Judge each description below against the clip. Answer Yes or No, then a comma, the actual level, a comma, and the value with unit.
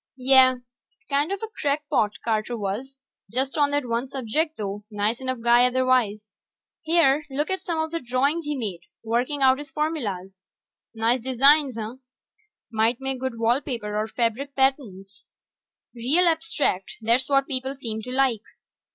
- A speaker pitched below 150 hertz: No, very high, 255 Hz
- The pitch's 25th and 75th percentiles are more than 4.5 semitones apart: No, average, 3.9 semitones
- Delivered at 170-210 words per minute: No, average, 155 wpm